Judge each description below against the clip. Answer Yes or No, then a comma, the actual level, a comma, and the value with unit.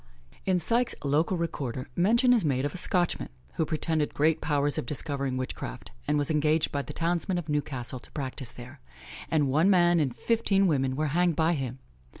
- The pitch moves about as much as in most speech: Yes, average, 3.9 semitones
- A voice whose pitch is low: No, medium, 155 Hz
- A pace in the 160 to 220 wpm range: Yes, average, 185 wpm